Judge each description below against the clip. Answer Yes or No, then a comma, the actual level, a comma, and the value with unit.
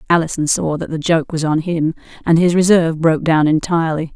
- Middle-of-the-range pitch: Yes, medium, 160 Hz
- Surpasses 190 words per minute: Yes, average, 200 wpm